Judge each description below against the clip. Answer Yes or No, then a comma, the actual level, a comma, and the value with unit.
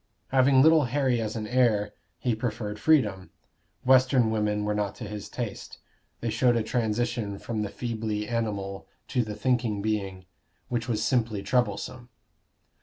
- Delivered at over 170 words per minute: No, average, 150 wpm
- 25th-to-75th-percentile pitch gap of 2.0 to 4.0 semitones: Yes, average, 2.9 semitones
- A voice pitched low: Yes, low, 115 Hz